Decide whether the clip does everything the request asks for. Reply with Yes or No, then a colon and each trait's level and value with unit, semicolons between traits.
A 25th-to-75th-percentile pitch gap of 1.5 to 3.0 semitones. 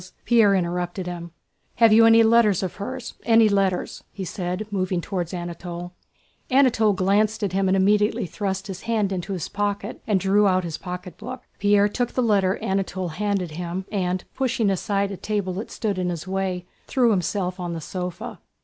Yes: narrow, 2.6 semitones